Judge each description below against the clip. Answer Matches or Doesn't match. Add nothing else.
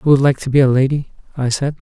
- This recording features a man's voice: Matches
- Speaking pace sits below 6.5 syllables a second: Doesn't match